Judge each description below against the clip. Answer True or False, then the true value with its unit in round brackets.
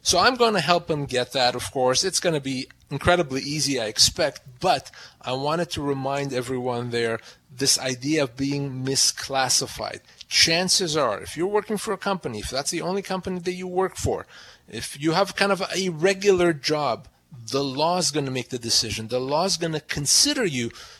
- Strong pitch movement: True (5.8 semitones)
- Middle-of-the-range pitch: True (145 Hz)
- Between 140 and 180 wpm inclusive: False (195 wpm)